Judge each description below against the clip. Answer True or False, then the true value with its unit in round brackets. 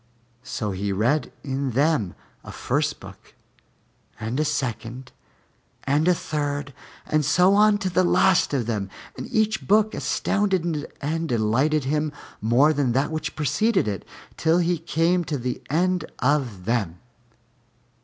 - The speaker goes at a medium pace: True (145 wpm)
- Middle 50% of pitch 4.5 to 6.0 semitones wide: True (5.5 semitones)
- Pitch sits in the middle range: True (150 Hz)